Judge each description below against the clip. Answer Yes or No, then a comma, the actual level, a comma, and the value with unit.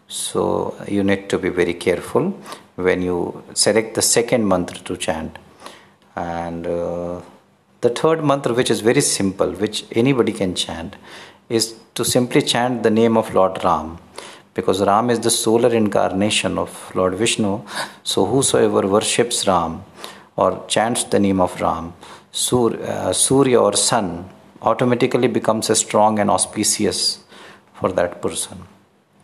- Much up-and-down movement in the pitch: No, average, 3.9 semitones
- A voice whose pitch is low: Yes, low, 105 Hz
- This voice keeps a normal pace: Yes, average, 145 wpm